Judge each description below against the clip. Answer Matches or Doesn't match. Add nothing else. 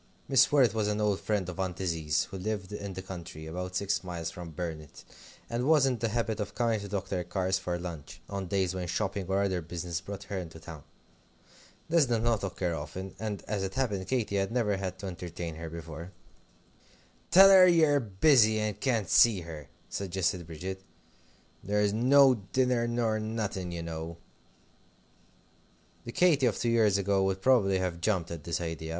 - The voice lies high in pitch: Doesn't match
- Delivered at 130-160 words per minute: Doesn't match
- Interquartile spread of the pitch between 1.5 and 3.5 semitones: Doesn't match